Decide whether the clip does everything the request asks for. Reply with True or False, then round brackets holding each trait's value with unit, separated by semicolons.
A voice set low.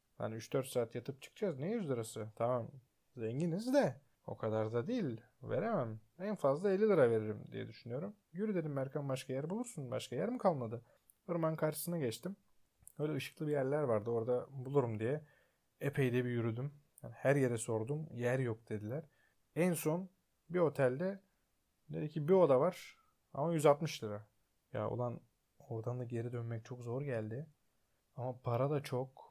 True (130 Hz)